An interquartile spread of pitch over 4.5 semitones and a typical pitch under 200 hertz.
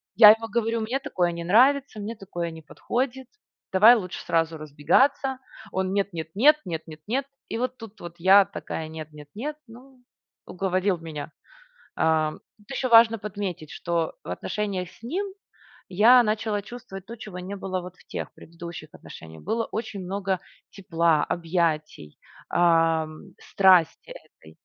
Yes: wide, 5.4 semitones; high, 190 Hz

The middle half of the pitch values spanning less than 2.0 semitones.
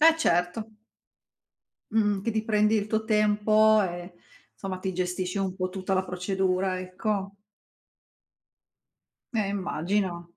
No: narrow, 2.6 semitones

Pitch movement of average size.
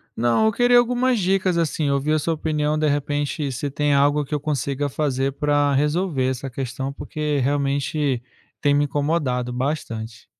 No: narrow, 2.2 semitones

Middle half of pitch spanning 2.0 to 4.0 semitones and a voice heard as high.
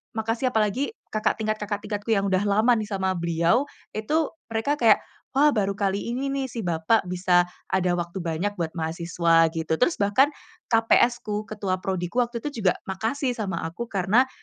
No: average, 4.5 semitones; high, 205 Hz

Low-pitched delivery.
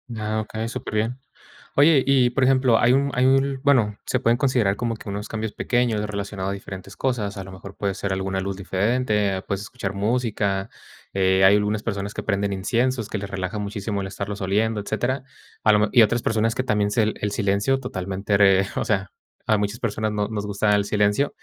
Yes: low, 105 Hz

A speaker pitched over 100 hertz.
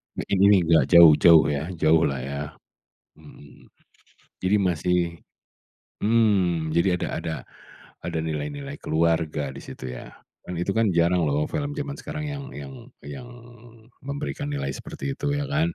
No: very low, 90 Hz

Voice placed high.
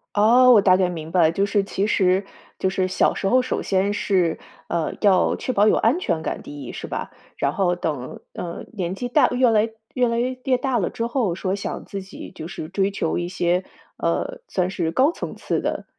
Yes: high, 195 Hz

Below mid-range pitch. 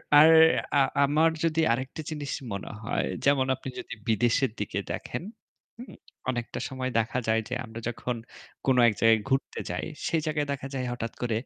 Yes: low, 130 Hz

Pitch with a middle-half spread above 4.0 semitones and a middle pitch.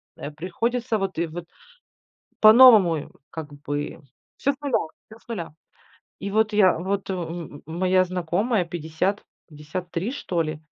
Yes: average, 4.9 semitones; medium, 180 Hz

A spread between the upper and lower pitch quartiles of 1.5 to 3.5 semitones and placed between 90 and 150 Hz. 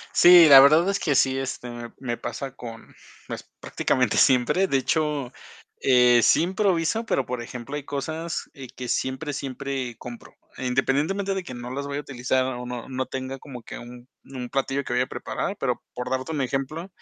Yes: average, 3.0 semitones; low, 135 Hz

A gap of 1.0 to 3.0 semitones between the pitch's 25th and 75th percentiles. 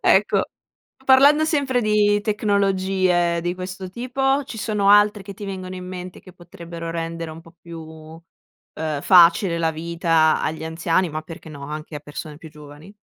No: average, 3.8 semitones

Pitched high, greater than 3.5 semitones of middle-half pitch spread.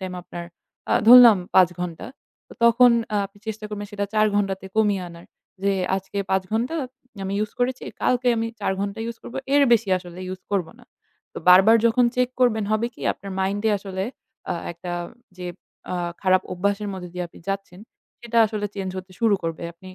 No: high, 200 Hz; average, 3.1 semitones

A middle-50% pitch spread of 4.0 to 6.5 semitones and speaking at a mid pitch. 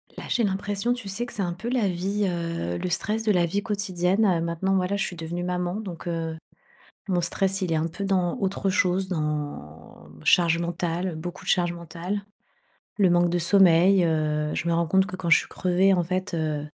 No: narrow, 2.5 semitones; medium, 180 Hz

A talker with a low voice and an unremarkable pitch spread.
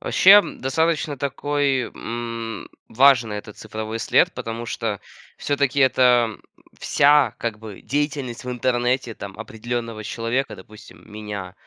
Yes: low, 120 Hz; average, 3.6 semitones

